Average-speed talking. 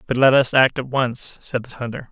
No: fast, 255 wpm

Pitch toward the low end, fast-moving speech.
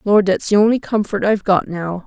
No: high, 200 Hz; fast, 230 wpm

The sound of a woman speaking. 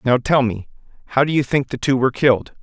No: male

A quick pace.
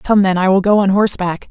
Yes: fast, 280 wpm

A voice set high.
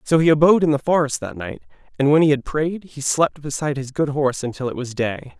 No: medium, 145 Hz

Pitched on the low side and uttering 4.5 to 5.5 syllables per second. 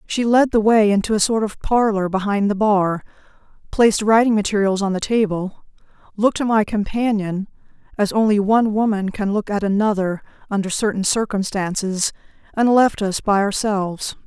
No: high, 205 Hz; 5.2 syllables/s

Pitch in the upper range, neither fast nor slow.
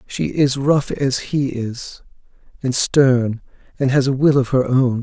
No: low, 130 Hz; average, 180 wpm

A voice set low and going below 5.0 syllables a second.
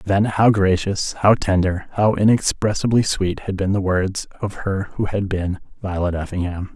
Yes: very low, 95 Hz; 4.5 syllables/s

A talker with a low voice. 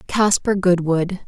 No: medium, 185 Hz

